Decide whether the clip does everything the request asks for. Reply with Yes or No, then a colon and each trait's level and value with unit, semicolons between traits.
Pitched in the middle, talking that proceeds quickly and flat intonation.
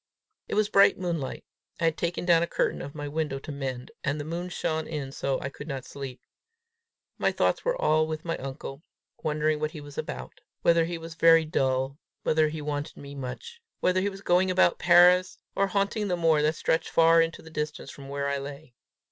No: medium, 155 Hz; fast, 215 wpm; average, 3.3 semitones